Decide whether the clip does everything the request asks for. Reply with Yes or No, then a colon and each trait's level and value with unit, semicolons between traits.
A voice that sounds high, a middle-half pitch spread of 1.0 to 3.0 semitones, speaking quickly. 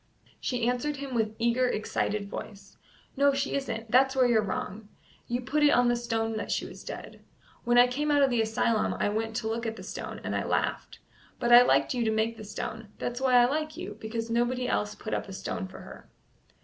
Yes: high, 240 Hz; narrow, 2.4 semitones; fast, 230 wpm